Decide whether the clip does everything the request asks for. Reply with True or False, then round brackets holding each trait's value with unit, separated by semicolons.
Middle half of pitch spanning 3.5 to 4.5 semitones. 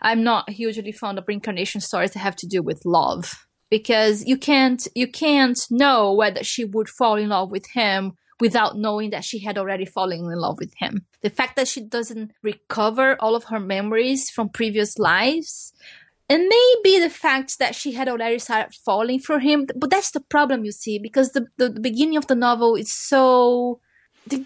True (4.0 semitones)